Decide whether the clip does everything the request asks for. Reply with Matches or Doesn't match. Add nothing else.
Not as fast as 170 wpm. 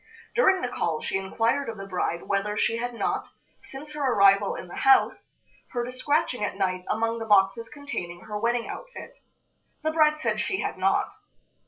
Doesn't match